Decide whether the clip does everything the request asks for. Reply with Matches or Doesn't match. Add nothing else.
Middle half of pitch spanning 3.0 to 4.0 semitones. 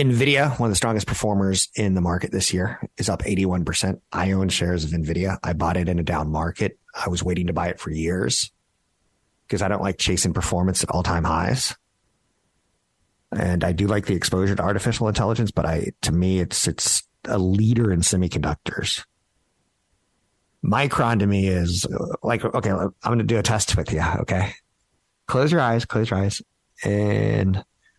Matches